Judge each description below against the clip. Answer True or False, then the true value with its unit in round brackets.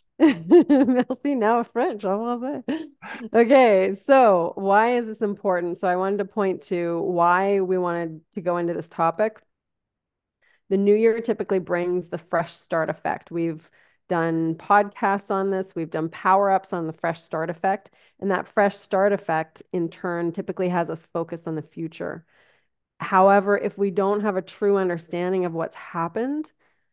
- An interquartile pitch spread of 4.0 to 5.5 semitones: False (3.5 semitones)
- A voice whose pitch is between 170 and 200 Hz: True (190 Hz)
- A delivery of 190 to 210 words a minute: False (165 wpm)